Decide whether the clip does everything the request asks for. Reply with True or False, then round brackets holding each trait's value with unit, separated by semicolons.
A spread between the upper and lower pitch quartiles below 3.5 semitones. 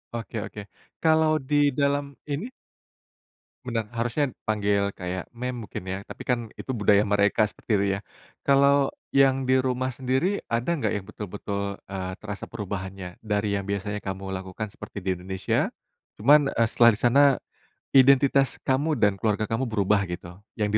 False (5.3 semitones)